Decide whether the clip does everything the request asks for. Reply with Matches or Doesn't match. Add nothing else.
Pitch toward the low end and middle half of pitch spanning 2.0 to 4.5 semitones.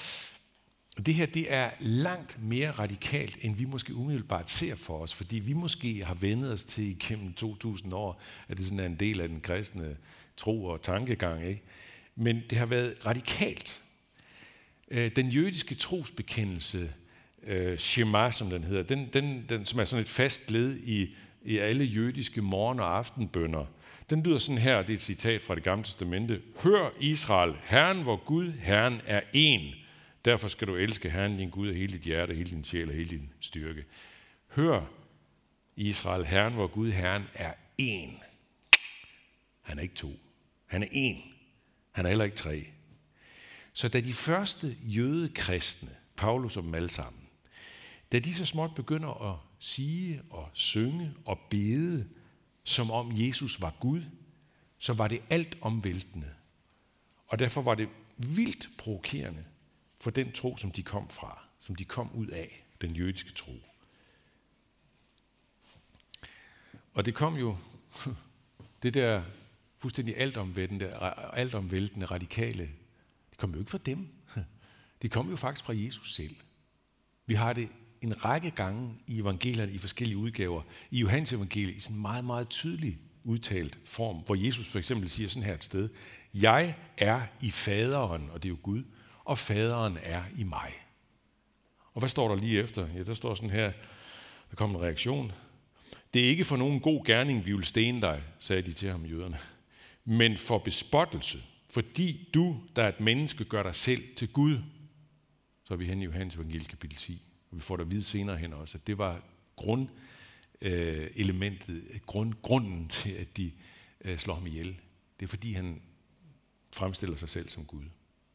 Doesn't match